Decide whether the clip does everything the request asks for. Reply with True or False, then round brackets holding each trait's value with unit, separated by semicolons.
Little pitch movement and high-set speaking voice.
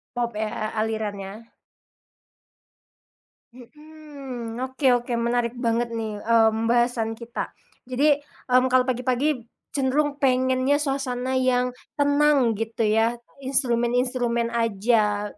True (2.3 semitones; 245 Hz)